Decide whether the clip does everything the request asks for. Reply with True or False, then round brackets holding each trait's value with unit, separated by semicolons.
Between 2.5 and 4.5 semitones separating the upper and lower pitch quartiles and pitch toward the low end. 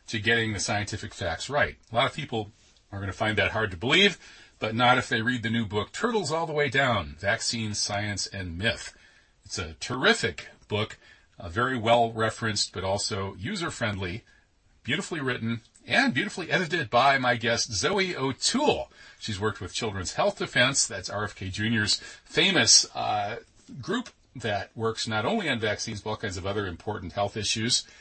True (2.8 semitones; 110 Hz)